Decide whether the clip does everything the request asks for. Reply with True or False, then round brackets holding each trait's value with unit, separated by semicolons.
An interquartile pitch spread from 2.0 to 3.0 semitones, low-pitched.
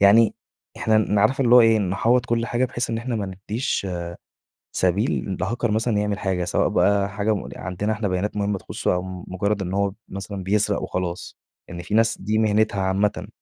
True (2.5 semitones; 105 Hz)